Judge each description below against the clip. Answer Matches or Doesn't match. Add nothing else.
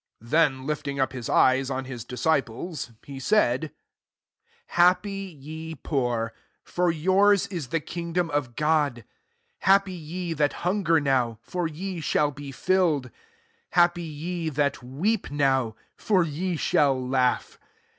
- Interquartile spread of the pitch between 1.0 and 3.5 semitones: Doesn't match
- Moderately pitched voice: Matches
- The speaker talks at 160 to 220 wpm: Doesn't match